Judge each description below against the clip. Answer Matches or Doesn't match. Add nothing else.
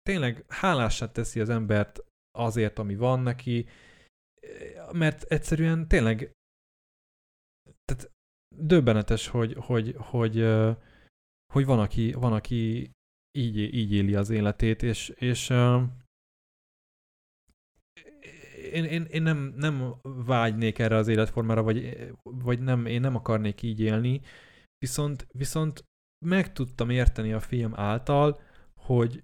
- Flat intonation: Doesn't match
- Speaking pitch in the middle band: Doesn't match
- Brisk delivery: Doesn't match